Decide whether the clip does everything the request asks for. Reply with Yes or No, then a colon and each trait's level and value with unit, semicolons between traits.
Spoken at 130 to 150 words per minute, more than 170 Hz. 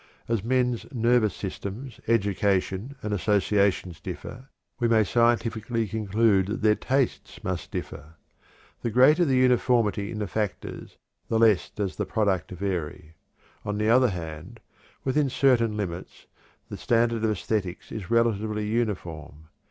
No: slow, 135 wpm; low, 110 Hz